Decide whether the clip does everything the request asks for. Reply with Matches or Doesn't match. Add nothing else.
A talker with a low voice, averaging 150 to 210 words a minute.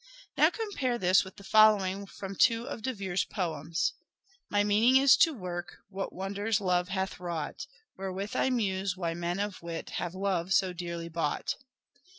Doesn't match